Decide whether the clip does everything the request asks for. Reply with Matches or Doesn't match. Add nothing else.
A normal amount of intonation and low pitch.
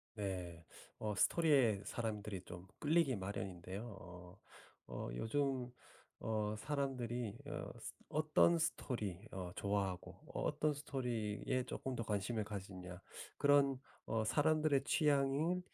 Doesn't match